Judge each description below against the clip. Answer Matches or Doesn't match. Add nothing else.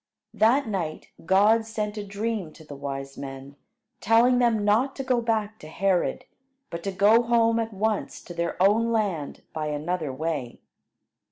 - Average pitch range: Doesn't match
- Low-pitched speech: Doesn't match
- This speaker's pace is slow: Doesn't match